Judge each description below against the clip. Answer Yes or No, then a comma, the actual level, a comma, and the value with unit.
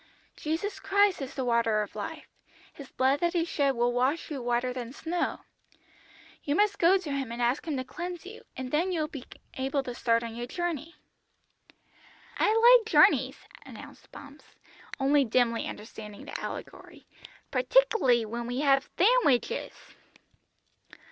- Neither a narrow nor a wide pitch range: No, wide, 6.0 semitones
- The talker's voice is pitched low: No, very high, 275 Hz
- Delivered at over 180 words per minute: No, average, 155 wpm